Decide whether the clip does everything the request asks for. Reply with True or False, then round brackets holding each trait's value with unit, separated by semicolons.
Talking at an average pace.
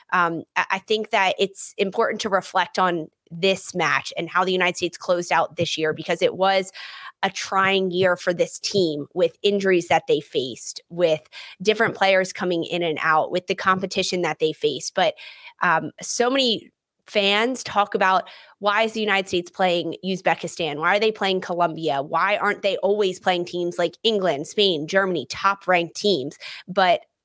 True (175 wpm)